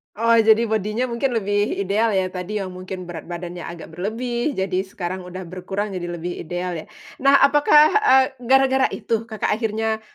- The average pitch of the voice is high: Yes, high, 205 Hz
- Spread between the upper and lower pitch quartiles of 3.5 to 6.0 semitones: Yes, average, 4.2 semitones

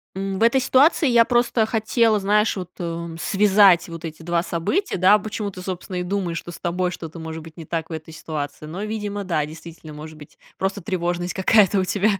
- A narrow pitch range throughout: No, average, 3.9 semitones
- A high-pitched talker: No, medium, 180 Hz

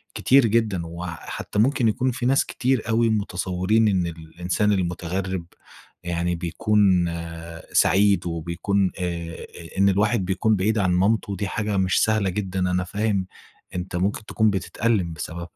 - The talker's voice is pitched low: Yes, very low, 95 Hz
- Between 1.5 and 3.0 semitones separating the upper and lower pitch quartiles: No, average, 3.4 semitones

